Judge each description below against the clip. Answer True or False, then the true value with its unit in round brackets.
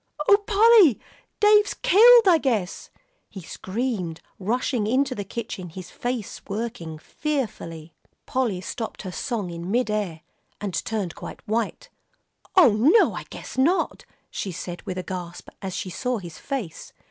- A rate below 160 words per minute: True (145 wpm)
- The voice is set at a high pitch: True (215 Hz)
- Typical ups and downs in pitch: False (6.3 semitones)